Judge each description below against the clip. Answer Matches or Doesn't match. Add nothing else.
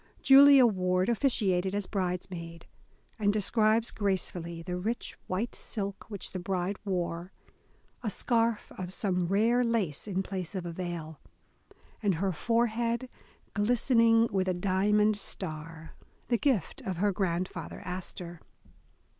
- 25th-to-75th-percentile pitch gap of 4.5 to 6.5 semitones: Doesn't match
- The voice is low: Doesn't match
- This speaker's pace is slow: Matches